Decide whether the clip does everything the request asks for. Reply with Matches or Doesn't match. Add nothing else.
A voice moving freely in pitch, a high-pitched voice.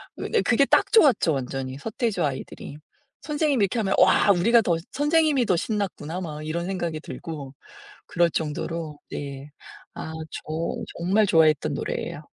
Doesn't match